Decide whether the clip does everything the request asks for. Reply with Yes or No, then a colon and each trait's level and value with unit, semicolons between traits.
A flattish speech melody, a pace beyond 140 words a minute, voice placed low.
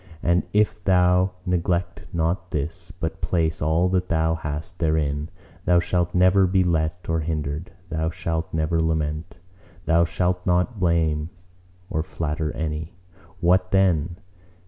No: narrow, 2.2 semitones; slow, 135 wpm; very low, 85 Hz